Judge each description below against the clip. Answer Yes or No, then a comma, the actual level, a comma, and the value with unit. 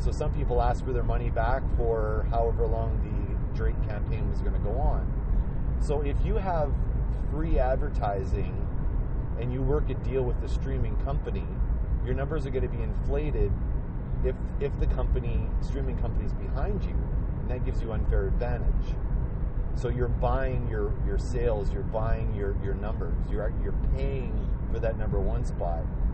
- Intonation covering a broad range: Yes, wide, 6.9 semitones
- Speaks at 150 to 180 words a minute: Yes, average, 170 wpm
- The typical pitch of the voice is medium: No, low, 105 Hz